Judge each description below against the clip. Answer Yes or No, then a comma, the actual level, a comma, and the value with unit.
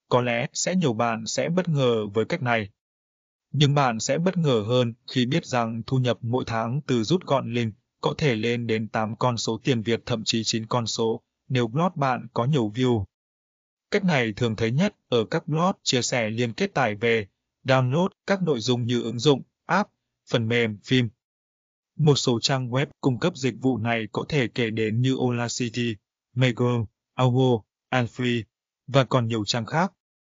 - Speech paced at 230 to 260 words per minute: No, average, 190 wpm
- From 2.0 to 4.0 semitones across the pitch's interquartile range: Yes, average, 3.1 semitones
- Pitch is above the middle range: No, low, 120 Hz